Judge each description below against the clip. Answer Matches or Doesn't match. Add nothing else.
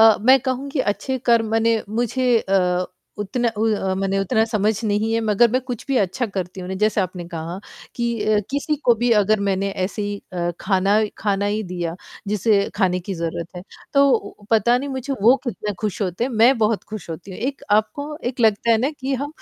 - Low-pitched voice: Doesn't match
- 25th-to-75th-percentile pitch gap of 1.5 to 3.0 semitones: Doesn't match